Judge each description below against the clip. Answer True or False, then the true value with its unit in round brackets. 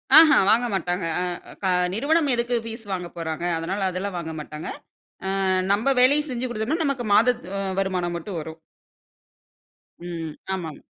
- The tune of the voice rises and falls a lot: True (6.0 semitones)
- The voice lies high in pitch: True (195 Hz)